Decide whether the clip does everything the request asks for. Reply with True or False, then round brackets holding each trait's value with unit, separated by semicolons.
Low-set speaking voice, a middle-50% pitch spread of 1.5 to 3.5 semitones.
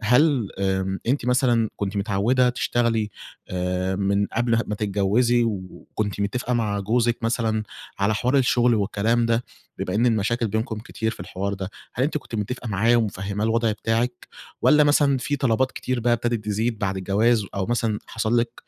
True (115 Hz; 3.0 semitones)